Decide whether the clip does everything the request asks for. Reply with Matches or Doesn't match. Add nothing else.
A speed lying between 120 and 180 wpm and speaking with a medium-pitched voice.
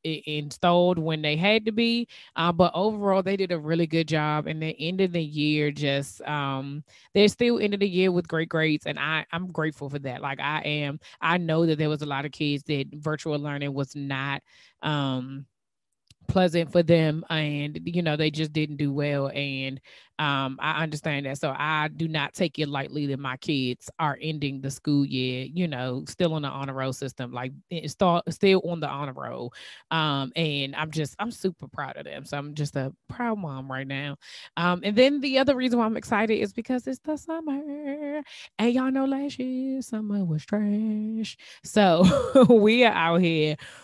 Doesn't match